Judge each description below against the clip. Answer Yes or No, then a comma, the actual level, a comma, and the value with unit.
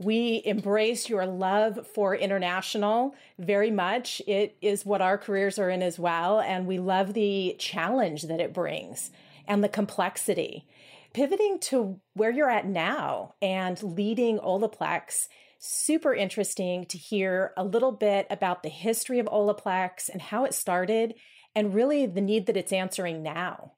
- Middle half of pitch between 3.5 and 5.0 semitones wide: No, average, 2.9 semitones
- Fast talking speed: No, average, 155 wpm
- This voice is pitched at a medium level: No, high, 200 Hz